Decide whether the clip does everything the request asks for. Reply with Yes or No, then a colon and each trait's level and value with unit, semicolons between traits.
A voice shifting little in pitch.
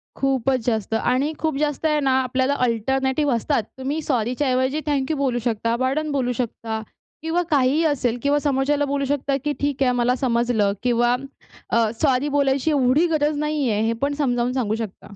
No: average, 3.0 semitones